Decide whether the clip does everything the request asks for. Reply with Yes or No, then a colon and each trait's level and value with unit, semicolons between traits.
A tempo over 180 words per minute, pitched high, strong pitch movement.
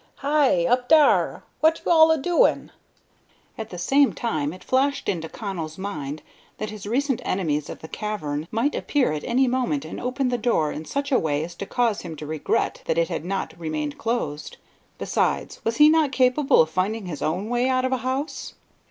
Yes: average, 200 wpm; high, 230 Hz; wide, 8.7 semitones